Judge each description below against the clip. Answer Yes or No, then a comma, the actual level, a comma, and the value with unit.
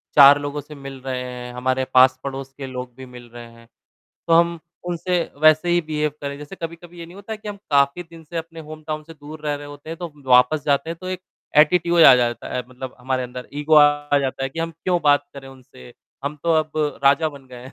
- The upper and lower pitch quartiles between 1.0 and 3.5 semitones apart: No, average, 3.9 semitones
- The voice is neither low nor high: Yes, medium, 145 Hz